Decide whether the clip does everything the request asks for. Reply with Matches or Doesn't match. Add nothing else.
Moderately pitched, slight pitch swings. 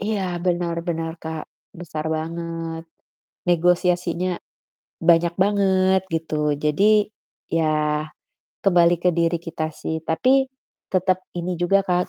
Matches